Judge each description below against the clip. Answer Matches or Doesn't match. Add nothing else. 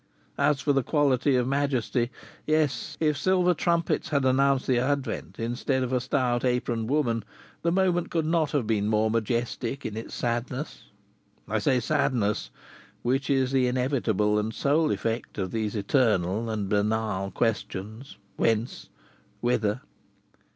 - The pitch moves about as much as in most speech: Matches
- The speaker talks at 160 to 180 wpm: Doesn't match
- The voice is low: Matches